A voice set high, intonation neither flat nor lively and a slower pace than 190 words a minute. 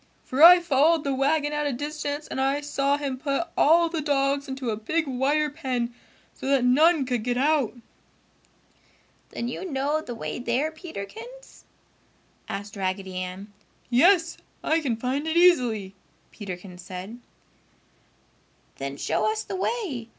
Yes: very high, 275 Hz; average, 4.9 semitones; average, 150 wpm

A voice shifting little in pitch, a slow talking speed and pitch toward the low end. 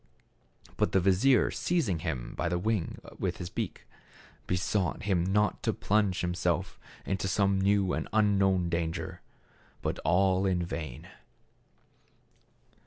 Yes: narrow, 2.3 semitones; slow, 130 wpm; very low, 95 Hz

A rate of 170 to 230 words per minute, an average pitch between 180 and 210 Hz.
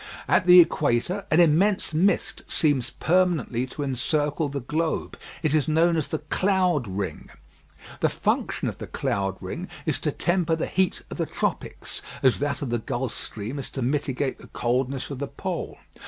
No: average, 175 wpm; medium, 145 Hz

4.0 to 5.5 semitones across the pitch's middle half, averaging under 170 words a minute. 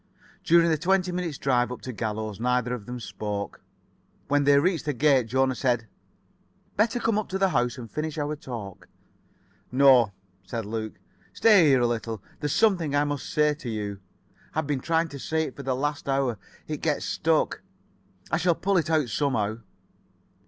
No: average, 4.7 semitones; average, 180 wpm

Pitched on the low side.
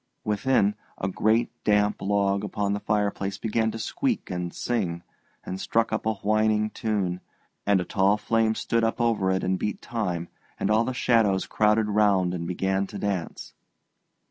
Yes: low, 105 Hz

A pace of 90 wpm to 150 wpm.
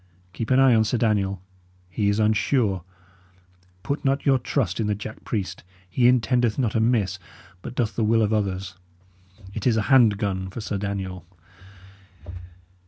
No: average, 165 wpm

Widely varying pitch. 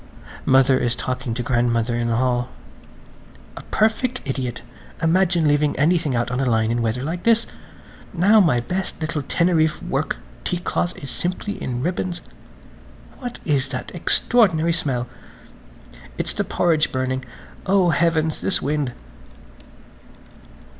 Yes: wide, 5.8 semitones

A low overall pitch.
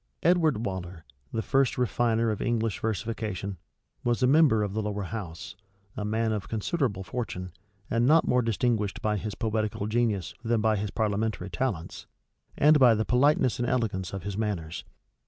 Yes: low, 110 Hz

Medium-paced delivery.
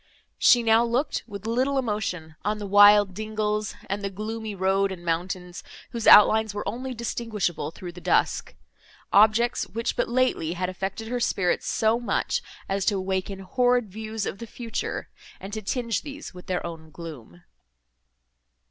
Yes: average, 155 wpm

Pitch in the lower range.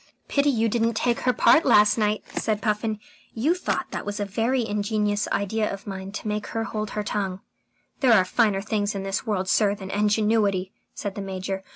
No: high, 210 Hz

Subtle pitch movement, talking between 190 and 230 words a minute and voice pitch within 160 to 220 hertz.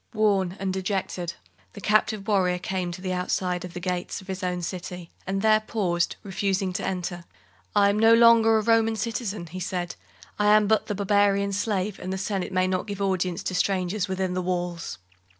Yes: narrow, 2.3 semitones; average, 195 wpm; high, 190 Hz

